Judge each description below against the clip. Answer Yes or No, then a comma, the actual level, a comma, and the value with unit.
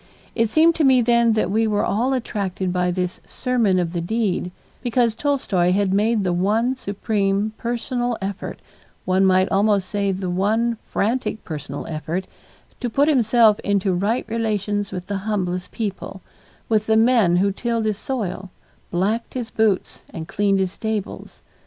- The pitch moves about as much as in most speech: Yes, average, 3.5 semitones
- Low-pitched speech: No, high, 205 Hz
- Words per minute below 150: No, average, 160 wpm